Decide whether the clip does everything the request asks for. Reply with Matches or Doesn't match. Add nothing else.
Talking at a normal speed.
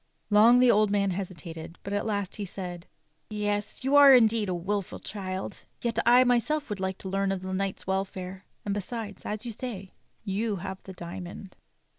Matches